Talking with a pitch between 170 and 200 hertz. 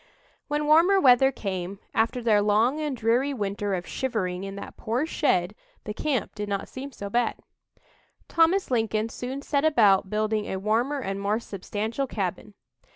No: high, 225 Hz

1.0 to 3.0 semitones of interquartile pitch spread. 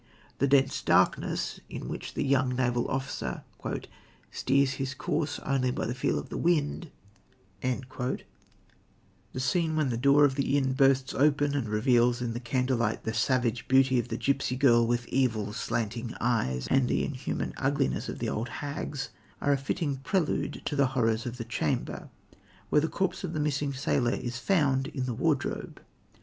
Yes: average, 2.7 semitones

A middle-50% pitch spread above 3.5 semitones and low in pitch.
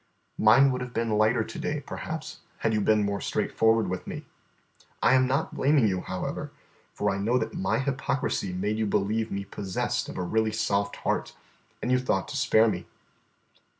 Yes: average, 3.9 semitones; low, 110 Hz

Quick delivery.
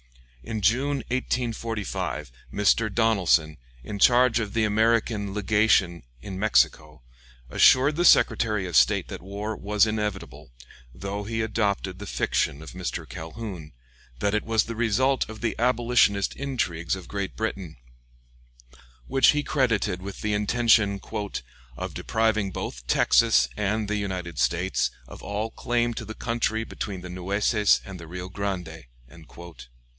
No: average, 140 wpm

